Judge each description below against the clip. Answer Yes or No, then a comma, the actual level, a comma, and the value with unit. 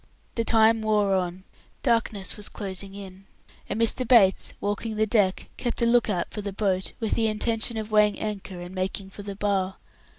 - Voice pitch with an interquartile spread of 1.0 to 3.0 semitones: Yes, narrow, 2.4 semitones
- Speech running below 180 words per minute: No, average, 190 wpm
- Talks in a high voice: Yes, high, 205 Hz